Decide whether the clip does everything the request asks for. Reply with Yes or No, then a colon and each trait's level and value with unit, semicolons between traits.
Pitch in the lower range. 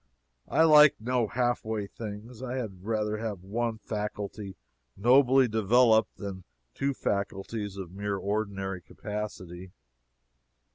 Yes: low, 105 Hz